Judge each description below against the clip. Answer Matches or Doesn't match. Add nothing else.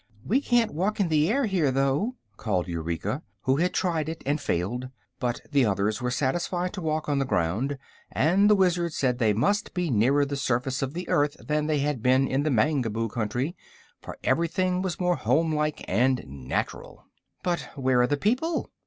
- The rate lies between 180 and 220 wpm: Matches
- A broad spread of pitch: Matches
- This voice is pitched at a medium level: Matches